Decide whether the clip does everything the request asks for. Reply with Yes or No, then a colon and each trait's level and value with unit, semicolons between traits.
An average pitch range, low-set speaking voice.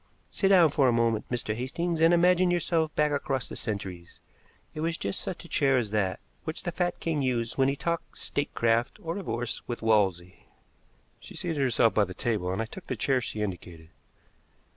No: wide, 7.2 semitones; low, 130 Hz